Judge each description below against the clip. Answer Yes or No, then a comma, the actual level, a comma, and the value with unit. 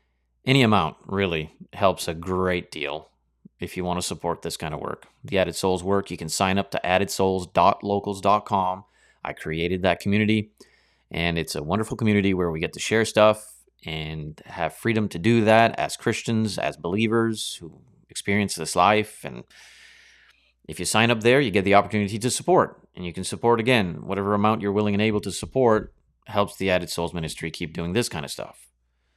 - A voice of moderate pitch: No, low, 100 Hz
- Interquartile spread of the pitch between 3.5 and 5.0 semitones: Yes, average, 4.0 semitones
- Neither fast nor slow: Yes, average, 185 wpm